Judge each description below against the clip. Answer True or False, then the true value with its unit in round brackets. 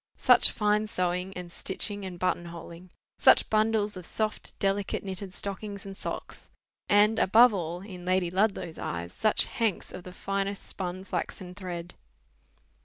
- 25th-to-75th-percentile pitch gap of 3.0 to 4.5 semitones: False (2.4 semitones)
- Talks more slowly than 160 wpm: True (150 wpm)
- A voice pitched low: False (190 Hz)